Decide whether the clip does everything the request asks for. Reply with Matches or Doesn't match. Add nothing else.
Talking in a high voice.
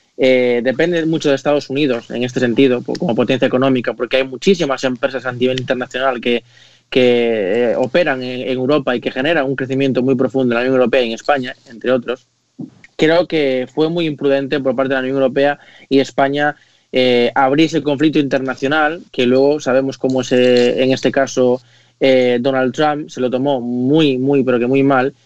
Doesn't match